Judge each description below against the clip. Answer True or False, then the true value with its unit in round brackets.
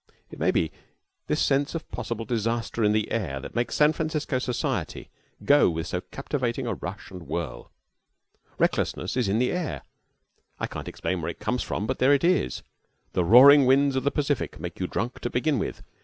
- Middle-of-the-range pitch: False (120 Hz)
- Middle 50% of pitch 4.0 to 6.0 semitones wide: True (5.4 semitones)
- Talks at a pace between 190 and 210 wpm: True (195 wpm)